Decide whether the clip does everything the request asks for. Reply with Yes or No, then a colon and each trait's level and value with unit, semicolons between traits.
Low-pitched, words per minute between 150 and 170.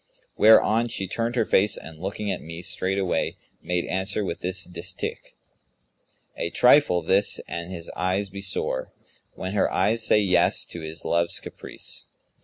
Yes: very low, 95 Hz; average, 160 wpm